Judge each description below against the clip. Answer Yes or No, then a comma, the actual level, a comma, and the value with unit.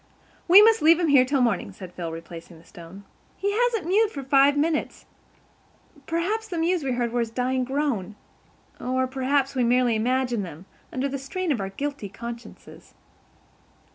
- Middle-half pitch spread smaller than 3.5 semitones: No, wide, 5.6 semitones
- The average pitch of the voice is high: Yes, very high, 260 Hz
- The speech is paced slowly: No, average, 170 wpm